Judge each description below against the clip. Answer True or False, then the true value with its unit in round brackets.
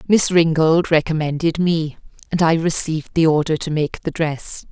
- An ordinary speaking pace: True (165 wpm)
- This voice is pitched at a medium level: True (160 Hz)